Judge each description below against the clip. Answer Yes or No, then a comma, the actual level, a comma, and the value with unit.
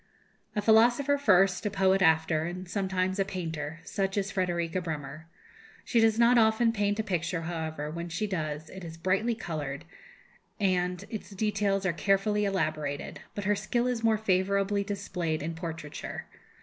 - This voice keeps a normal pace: Yes, average, 160 wpm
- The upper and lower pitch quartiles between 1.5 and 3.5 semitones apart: No, average, 3.9 semitones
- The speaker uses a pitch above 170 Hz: Yes, high, 190 Hz